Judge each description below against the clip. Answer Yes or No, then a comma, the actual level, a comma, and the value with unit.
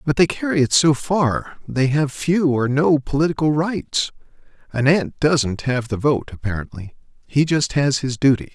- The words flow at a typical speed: Yes, average, 175 wpm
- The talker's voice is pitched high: No, medium, 140 Hz